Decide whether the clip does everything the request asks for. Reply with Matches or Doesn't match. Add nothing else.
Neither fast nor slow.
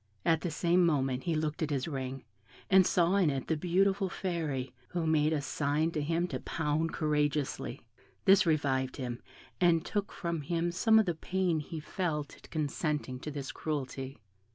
Matches